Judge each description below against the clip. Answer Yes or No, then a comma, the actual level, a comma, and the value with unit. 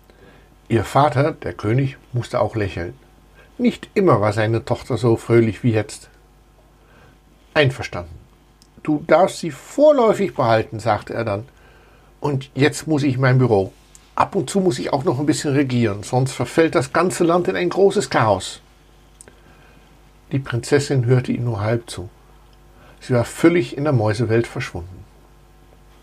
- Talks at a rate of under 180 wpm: Yes, average, 150 wpm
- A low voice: Yes, low, 125 Hz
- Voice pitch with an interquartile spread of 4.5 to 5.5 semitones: Yes, average, 5.2 semitones